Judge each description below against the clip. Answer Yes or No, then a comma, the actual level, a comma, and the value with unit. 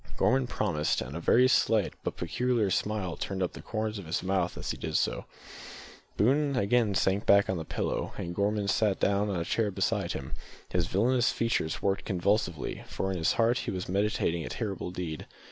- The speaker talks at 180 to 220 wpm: Yes, average, 195 wpm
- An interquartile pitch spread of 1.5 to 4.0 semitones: Yes, average, 3.6 semitones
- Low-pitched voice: Yes, low, 100 Hz